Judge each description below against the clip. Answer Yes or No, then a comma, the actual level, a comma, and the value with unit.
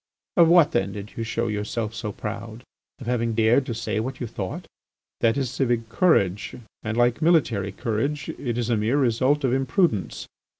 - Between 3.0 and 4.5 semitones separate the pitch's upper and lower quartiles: Yes, average, 3.4 semitones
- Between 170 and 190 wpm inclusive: Yes, average, 180 wpm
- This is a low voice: Yes, low, 115 Hz